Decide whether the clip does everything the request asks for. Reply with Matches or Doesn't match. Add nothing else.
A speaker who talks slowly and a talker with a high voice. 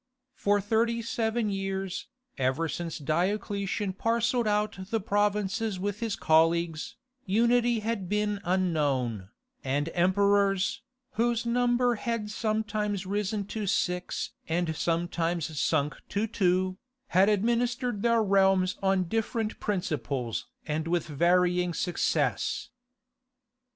Matches